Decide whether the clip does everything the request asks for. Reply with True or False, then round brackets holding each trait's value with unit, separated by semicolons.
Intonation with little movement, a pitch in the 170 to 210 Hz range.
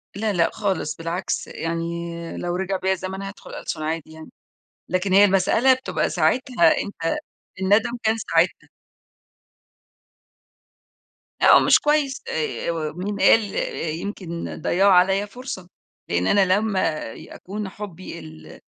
False (3.5 semitones; 190 Hz)